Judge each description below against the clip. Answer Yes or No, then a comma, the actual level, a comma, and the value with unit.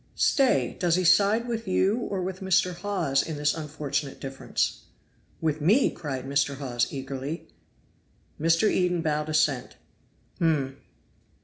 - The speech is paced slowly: Yes, slow, 130 wpm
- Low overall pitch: No, medium, 160 Hz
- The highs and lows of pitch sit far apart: No, average, 4.9 semitones